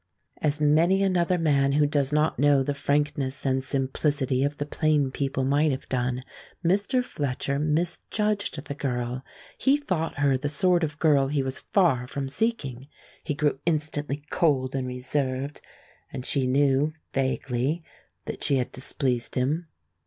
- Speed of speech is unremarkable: Yes, average, 155 wpm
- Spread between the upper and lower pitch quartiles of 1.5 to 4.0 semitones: Yes, average, 2.7 semitones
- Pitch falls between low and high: Yes, medium, 145 Hz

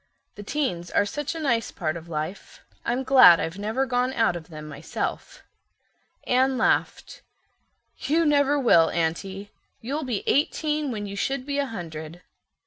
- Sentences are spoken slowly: No, average, 155 wpm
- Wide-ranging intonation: Yes, wide, 8.0 semitones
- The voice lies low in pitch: No, high, 225 Hz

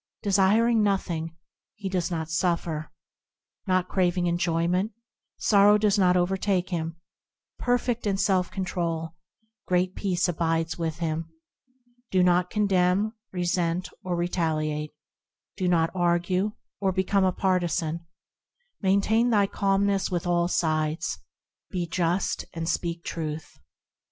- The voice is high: No, medium, 180 Hz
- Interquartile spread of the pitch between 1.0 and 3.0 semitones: Yes, narrow, 2.6 semitones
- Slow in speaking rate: Yes, slow, 115 wpm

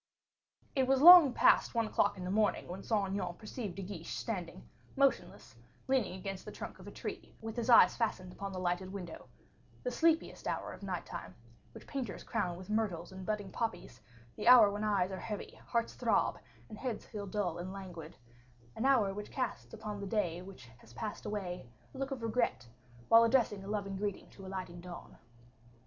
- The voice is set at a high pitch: Yes, high, 200 Hz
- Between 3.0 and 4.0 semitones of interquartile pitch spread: Yes, average, 3.6 semitones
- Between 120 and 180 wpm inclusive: No, average, 195 wpm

